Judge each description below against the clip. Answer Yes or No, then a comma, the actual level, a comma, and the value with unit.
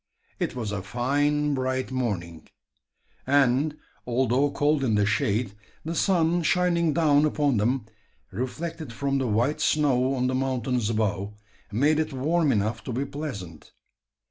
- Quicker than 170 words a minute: No, average, 145 wpm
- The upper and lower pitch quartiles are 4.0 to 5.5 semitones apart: Yes, average, 4.4 semitones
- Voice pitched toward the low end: Yes, low, 130 Hz